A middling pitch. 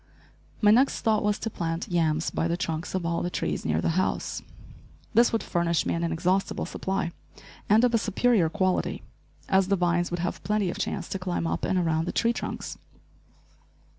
Yes: medium, 180 Hz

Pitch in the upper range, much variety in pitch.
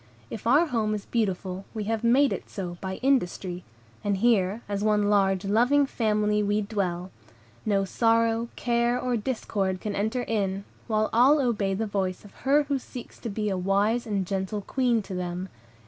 No: high, 210 Hz; average, 3.3 semitones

